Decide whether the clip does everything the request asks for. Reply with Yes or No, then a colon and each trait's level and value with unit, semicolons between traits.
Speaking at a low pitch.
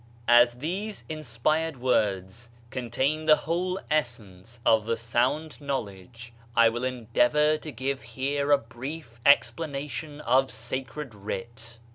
Yes: low, 130 Hz